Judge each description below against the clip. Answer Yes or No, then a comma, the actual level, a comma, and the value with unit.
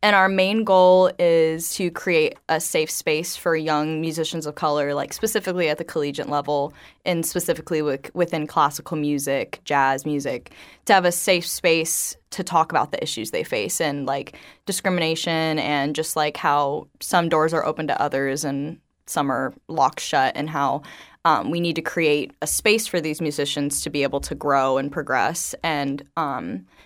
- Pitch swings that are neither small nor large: Yes, average, 3.3 semitones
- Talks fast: No, average, 180 wpm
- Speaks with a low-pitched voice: No, medium, 160 Hz